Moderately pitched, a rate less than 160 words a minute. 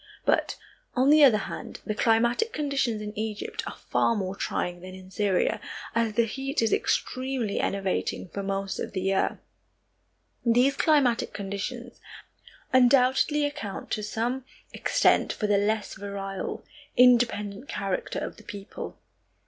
No: high, 220 Hz; average, 140 wpm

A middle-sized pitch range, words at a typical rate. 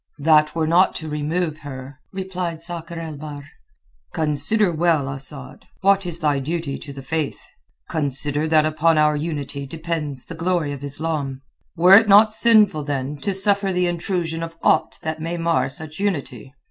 Yes: average, 3.2 semitones; average, 165 wpm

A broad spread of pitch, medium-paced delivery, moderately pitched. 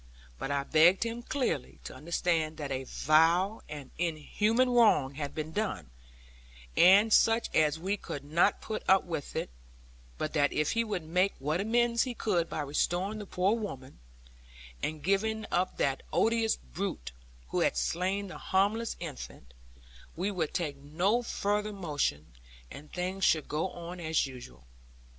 Yes: wide, 5.7 semitones; average, 155 wpm; medium, 175 Hz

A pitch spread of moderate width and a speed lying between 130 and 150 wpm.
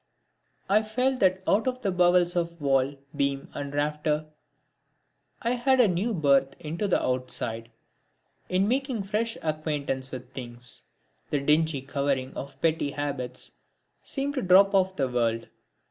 No: wide, 6.3 semitones; average, 145 wpm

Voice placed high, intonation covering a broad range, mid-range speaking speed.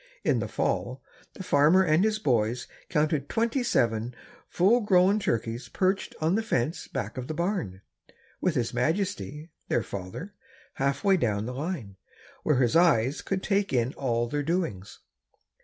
No: medium, 150 Hz; wide, 7.9 semitones; average, 155 wpm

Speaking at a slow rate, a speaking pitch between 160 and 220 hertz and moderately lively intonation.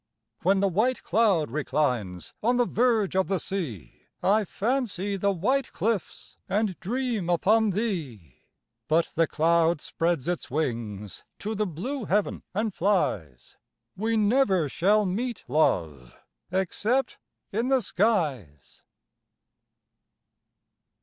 No: slow, 115 wpm; high, 190 Hz; wide, 5.9 semitones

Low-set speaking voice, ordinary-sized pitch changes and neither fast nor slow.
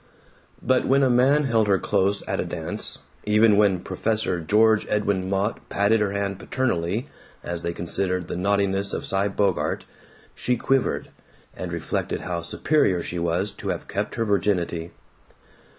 Yes: low, 100 Hz; average, 3.2 semitones; average, 155 wpm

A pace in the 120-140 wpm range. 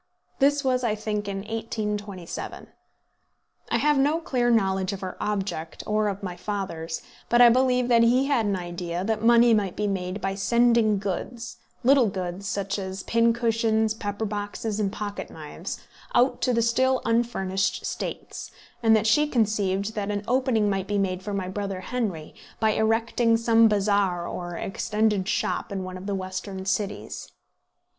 No: average, 165 wpm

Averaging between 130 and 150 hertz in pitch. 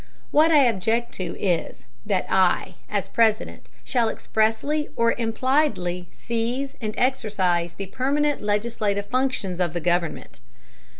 No: high, 225 Hz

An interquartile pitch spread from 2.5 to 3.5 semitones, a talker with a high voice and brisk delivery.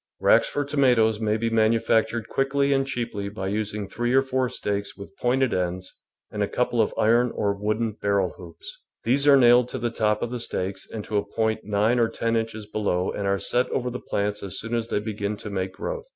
No: average, 3.1 semitones; low, 110 Hz; fast, 225 wpm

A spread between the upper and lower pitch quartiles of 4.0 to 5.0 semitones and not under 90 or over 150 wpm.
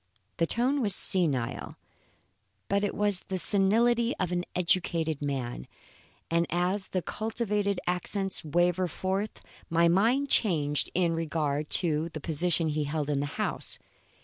Yes: average, 4.3 semitones; average, 140 wpm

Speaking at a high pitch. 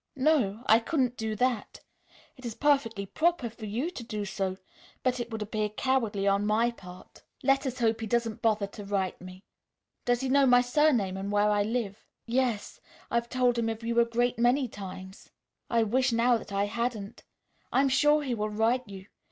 Yes: high, 230 Hz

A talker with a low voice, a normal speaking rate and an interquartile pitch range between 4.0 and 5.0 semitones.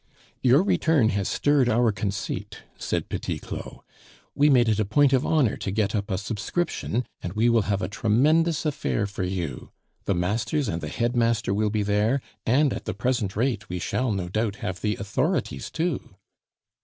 Yes: low, 110 Hz; average, 180 wpm; average, 4.7 semitones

